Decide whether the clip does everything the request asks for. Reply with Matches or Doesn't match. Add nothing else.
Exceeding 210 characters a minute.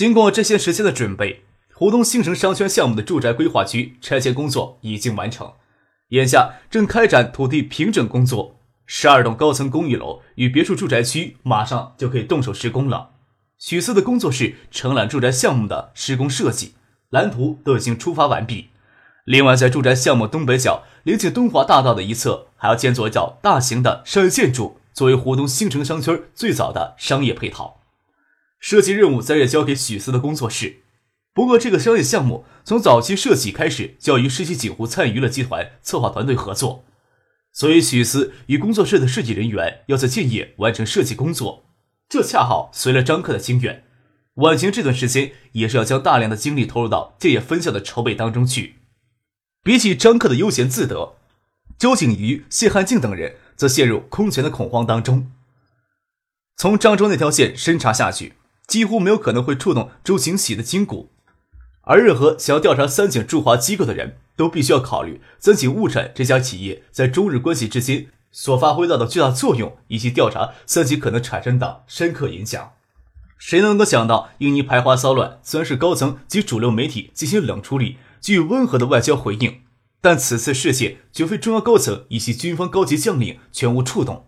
Matches